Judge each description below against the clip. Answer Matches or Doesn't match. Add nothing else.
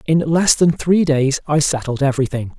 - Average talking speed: Matches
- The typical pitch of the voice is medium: Matches